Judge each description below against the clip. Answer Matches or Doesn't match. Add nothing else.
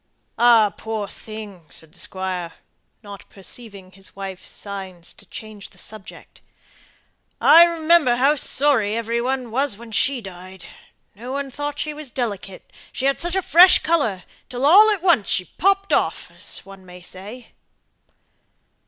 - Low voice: Doesn't match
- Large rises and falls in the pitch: Matches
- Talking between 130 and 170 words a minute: Matches